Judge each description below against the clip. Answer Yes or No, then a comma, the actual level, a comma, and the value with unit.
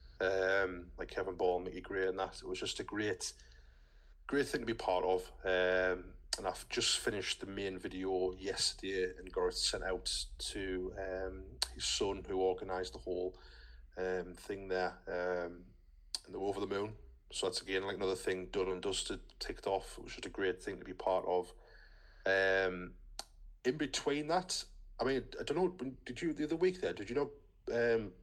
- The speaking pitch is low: Yes, very low, 95 Hz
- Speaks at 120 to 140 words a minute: No, average, 190 wpm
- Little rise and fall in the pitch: Yes, narrow, 1.4 semitones